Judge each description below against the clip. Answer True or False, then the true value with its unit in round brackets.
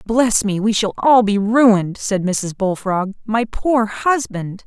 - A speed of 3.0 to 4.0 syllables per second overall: True (3.8 syllables/s)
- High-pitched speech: True (215 Hz)